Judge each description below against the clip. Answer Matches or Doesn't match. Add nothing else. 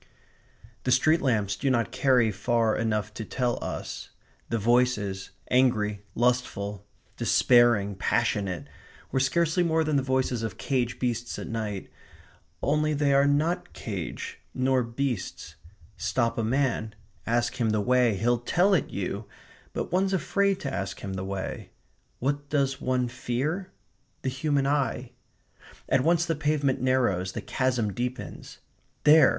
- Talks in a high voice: Doesn't match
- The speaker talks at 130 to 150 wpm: Matches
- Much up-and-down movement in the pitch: Doesn't match